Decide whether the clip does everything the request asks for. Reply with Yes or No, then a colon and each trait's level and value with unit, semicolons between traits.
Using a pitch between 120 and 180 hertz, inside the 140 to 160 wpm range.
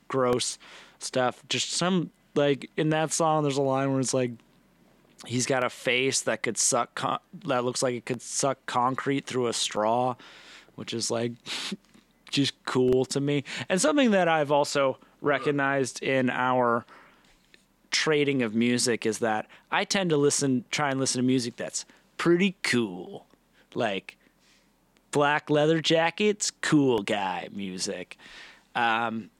Yes: low, 135 Hz; average, 145 wpm